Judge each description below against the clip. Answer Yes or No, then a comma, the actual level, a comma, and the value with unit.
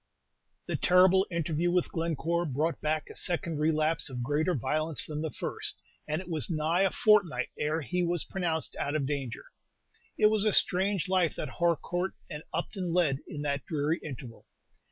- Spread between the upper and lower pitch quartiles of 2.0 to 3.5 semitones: Yes, average, 3.0 semitones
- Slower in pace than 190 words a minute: Yes, average, 175 wpm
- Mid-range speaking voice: Yes, medium, 160 Hz